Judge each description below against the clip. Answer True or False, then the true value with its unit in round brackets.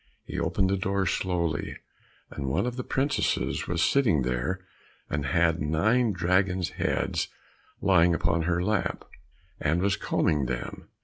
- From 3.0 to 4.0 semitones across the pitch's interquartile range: True (3.5 semitones)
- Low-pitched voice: True (90 Hz)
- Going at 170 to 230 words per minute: False (140 wpm)